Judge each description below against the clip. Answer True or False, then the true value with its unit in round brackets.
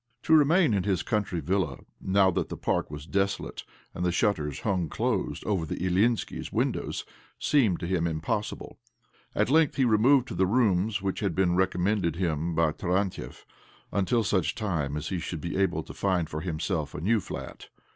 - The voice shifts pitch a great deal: False (3.8 semitones)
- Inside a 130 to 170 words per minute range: False (185 wpm)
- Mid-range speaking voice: False (95 Hz)